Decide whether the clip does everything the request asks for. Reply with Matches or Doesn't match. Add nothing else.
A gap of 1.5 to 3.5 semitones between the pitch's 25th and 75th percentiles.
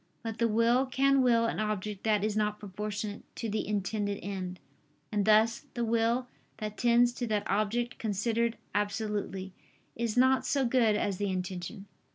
Matches